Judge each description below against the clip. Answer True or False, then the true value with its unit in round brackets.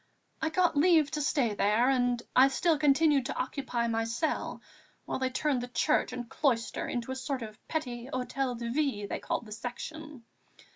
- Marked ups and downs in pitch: False (4.0 semitones)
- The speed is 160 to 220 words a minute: True (185 wpm)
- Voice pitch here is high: True (260 Hz)